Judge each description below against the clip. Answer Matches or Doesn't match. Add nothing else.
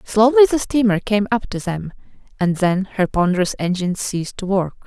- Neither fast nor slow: Matches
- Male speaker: Doesn't match